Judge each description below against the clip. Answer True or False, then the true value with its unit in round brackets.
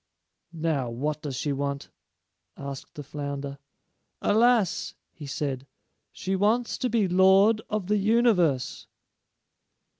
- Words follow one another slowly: True (115 wpm)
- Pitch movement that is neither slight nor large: False (7.0 semitones)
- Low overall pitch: False (160 Hz)